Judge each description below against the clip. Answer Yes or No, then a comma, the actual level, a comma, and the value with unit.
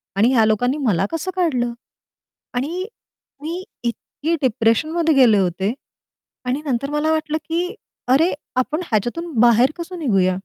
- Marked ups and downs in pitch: Yes, wide, 6.0 semitones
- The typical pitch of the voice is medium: No, very high, 265 Hz